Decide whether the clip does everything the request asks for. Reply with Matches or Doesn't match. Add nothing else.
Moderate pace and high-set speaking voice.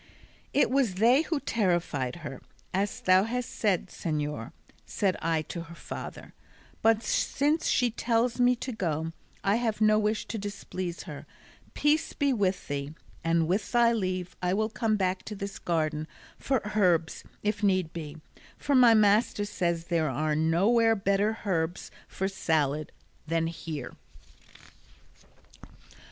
Matches